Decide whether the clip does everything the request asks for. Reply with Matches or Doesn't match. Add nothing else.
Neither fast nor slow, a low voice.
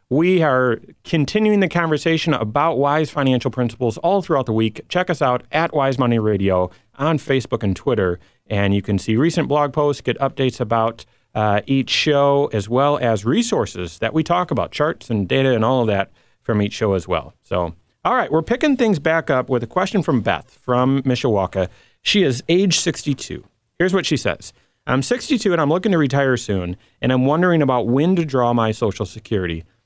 Matches